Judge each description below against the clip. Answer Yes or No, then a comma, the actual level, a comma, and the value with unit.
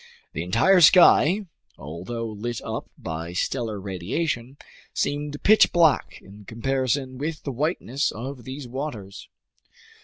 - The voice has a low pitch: Yes, low, 130 Hz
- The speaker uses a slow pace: Yes, slow, 120 wpm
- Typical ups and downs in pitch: No, wide, 5.8 semitones